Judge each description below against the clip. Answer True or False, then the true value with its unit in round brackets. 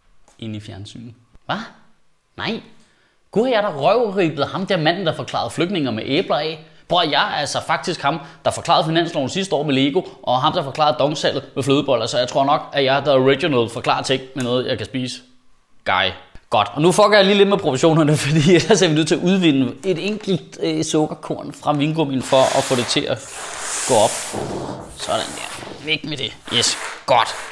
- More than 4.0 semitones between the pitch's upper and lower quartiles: True (4.4 semitones)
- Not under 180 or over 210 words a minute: True (205 wpm)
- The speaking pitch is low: False (150 Hz)